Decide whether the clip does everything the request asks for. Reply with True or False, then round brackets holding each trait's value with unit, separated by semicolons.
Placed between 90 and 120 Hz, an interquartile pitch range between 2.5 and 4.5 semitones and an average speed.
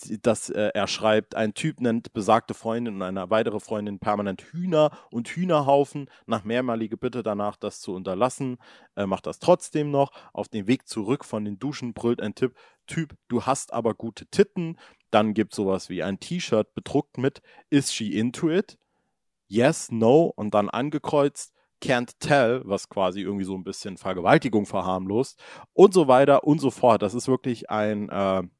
False (115 Hz; 4.9 semitones; 175 wpm)